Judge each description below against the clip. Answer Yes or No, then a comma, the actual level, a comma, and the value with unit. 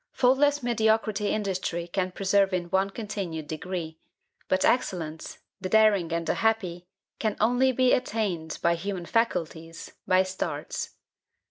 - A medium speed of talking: No, slow, 130 wpm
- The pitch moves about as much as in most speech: Yes, average, 4.2 semitones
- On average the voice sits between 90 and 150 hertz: No, high, 190 Hz